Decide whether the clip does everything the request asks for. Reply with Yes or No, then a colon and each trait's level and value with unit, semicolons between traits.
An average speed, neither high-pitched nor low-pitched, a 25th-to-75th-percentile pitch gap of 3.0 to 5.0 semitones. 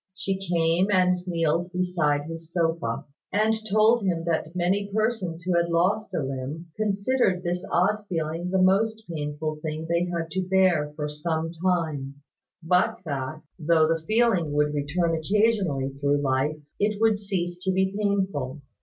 Yes: average, 155 wpm; medium, 170 Hz; average, 3.5 semitones